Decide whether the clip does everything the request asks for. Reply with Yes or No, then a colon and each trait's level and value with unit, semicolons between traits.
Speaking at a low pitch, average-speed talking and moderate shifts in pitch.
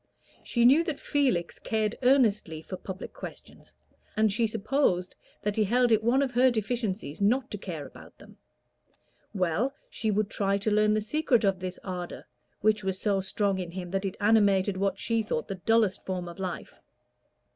No: high, 210 Hz; average, 180 wpm; average, 3.3 semitones